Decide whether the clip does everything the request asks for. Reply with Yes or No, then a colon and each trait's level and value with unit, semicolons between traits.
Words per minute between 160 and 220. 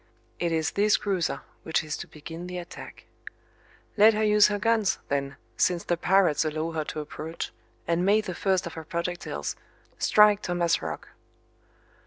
Yes: average, 165 wpm